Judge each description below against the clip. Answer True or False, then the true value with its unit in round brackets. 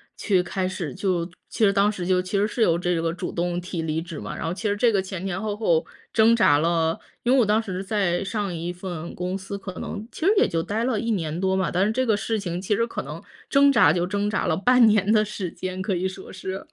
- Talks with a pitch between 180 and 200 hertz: True (190 Hz)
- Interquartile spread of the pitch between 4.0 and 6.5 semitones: False (3.2 semitones)